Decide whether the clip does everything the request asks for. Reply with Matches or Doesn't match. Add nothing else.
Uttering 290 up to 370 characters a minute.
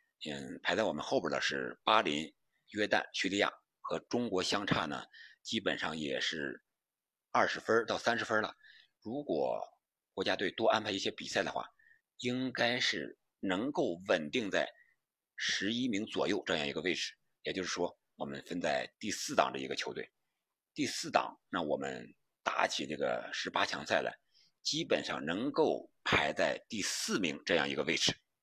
Doesn't match